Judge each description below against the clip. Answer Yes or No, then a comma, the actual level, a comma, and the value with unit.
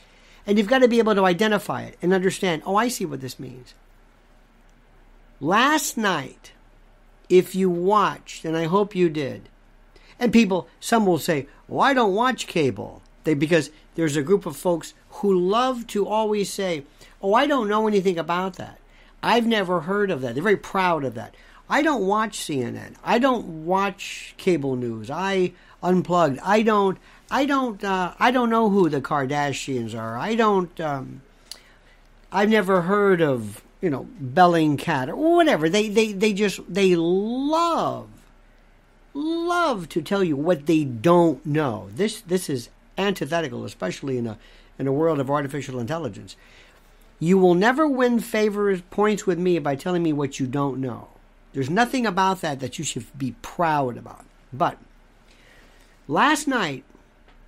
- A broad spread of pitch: Yes, wide, 6.4 semitones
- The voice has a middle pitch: Yes, medium, 180 Hz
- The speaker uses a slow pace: No, average, 165 wpm